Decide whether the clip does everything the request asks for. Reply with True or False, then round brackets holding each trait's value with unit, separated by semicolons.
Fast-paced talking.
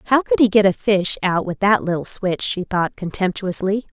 True (210 wpm)